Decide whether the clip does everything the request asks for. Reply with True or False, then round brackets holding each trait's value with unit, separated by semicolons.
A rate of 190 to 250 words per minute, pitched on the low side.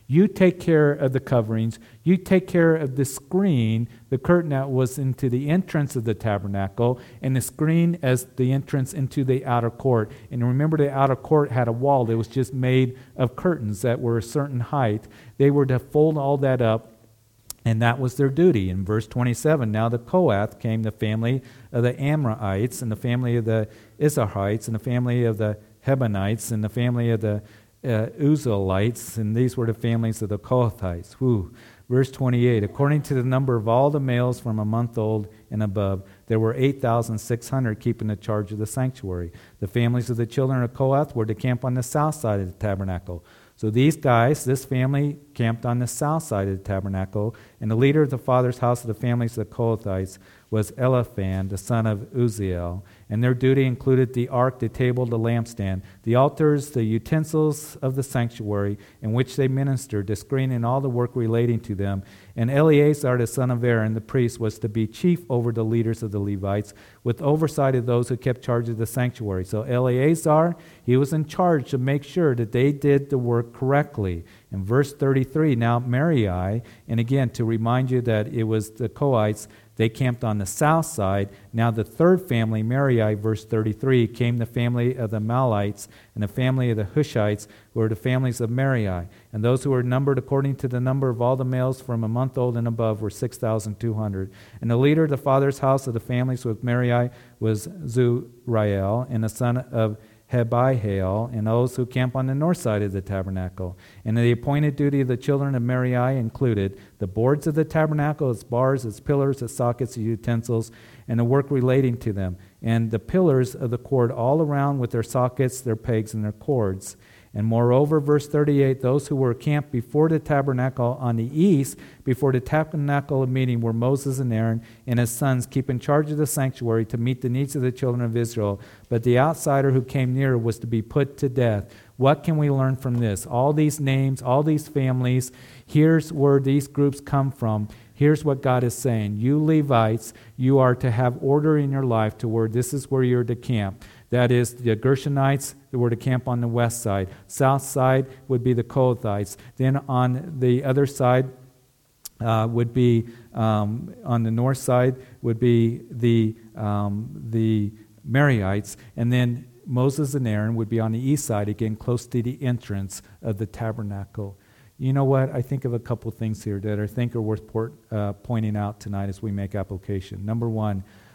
True (200 wpm; 120 Hz)